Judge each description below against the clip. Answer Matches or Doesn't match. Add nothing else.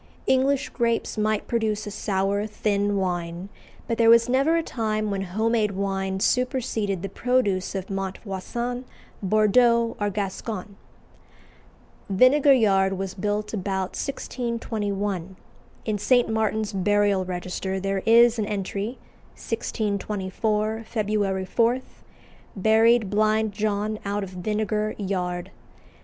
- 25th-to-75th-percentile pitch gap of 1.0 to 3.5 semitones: Matches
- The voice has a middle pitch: Doesn't match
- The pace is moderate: Doesn't match